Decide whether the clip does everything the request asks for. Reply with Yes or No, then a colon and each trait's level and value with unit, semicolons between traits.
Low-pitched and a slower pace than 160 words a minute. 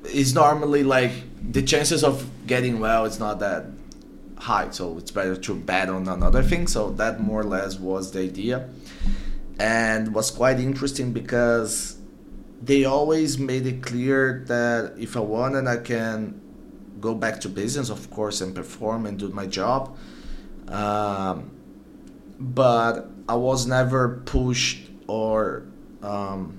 Yes: low, 115 Hz; average, 145 wpm